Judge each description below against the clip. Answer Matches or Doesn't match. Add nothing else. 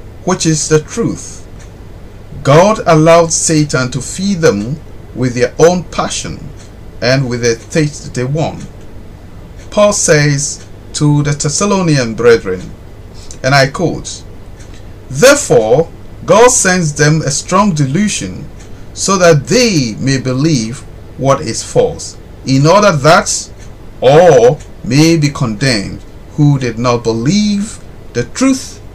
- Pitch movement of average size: Doesn't match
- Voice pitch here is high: Doesn't match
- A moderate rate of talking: Doesn't match